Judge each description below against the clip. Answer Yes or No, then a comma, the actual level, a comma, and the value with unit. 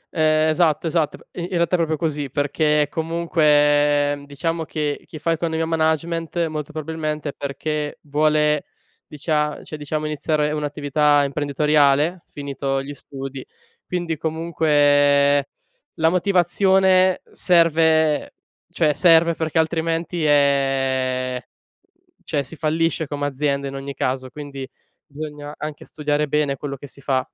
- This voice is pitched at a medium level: Yes, medium, 150 Hz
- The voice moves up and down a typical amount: No, narrow, 2.1 semitones